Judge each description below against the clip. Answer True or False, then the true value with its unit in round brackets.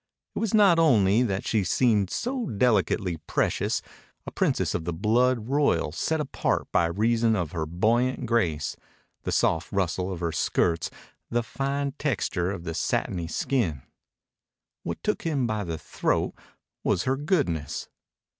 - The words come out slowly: False (150 wpm)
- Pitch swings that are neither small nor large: False (7.1 semitones)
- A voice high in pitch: False (105 Hz)